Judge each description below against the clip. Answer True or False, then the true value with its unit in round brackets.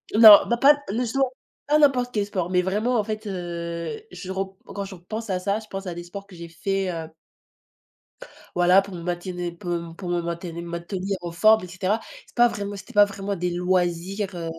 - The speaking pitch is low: False (190 Hz)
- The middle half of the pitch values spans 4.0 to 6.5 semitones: False (2.9 semitones)